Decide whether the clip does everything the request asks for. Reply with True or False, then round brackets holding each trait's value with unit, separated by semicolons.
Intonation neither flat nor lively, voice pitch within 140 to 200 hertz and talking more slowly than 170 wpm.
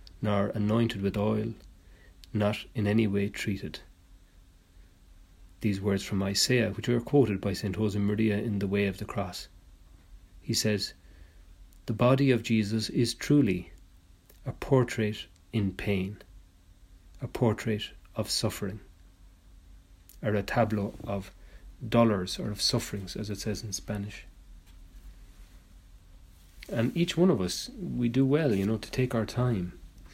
False (3.5 semitones; 100 Hz; 135 wpm)